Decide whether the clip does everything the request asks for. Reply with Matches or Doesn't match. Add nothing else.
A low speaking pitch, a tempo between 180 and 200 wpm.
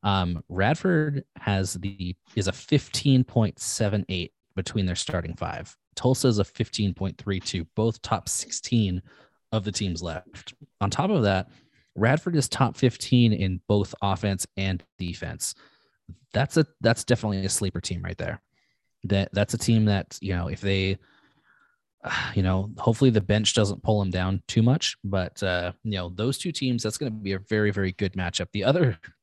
Doesn't match